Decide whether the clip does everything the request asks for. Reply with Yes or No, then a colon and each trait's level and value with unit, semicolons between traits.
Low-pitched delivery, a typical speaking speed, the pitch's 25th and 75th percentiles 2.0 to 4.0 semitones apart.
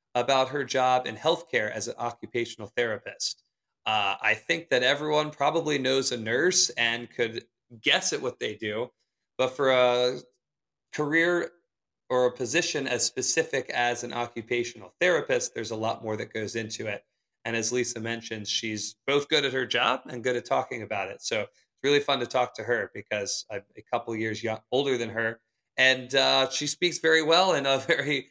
Yes: low, 125 Hz; average, 190 wpm; average, 3.4 semitones